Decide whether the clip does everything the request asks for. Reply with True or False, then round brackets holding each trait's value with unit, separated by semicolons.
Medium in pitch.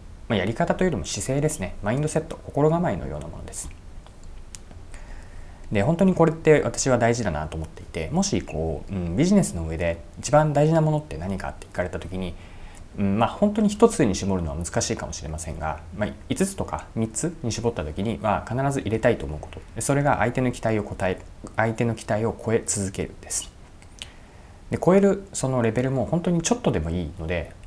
False (100 Hz)